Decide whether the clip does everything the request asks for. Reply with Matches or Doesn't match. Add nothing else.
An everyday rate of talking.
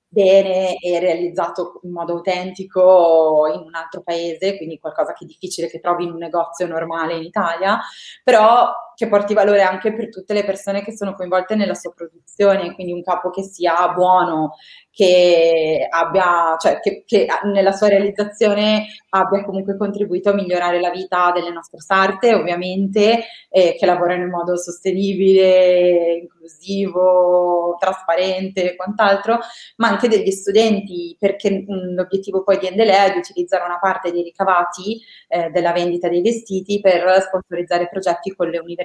Matches